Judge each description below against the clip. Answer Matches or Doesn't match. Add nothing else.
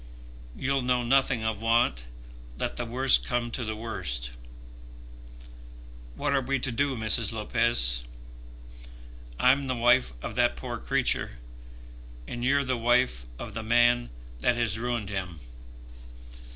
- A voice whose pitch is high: Doesn't match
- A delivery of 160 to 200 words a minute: Doesn't match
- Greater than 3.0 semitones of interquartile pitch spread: Doesn't match